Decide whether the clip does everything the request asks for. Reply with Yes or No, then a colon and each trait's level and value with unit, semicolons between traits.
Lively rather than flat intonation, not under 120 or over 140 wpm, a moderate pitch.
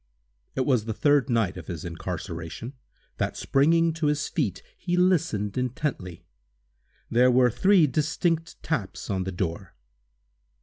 No: wide, 8.0 semitones; slow, 135 wpm; low, 125 Hz